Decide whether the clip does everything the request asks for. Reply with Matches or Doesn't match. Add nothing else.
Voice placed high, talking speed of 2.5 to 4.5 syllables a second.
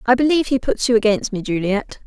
Doesn't match